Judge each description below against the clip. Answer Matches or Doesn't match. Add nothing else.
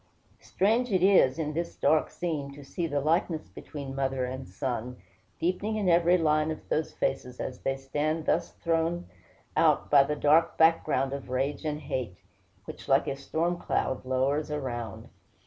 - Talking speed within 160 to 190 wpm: Matches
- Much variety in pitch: Doesn't match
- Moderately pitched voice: Matches